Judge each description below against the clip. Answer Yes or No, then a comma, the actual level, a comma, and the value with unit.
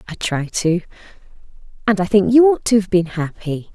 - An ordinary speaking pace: Yes, average, 190 wpm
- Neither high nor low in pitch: No, high, 195 Hz